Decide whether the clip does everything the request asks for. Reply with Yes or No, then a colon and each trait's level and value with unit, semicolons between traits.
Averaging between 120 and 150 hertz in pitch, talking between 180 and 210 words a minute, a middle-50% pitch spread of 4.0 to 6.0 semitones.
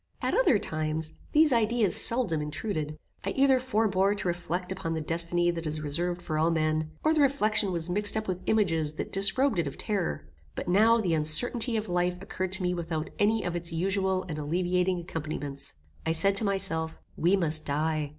No: medium, 180 Hz; average, 190 wpm; average, 4.4 semitones